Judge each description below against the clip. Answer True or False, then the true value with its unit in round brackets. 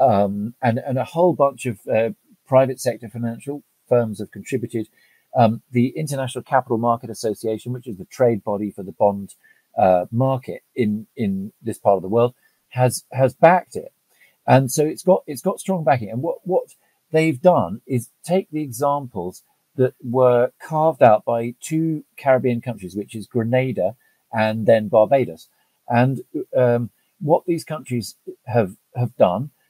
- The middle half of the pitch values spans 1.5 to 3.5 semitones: False (4.1 semitones)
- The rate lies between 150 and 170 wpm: True (160 wpm)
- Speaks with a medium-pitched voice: False (125 Hz)